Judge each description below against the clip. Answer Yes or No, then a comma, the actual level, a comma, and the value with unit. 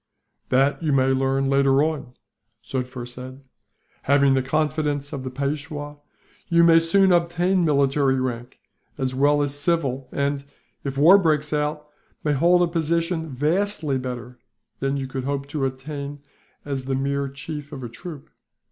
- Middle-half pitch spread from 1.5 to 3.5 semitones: Yes, narrow, 2.6 semitones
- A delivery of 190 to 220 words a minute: No, average, 155 wpm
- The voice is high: No, medium, 140 Hz